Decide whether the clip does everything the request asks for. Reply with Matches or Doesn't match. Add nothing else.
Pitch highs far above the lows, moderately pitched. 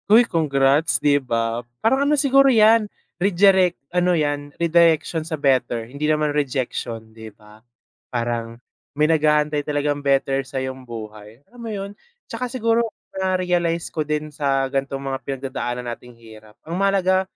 Matches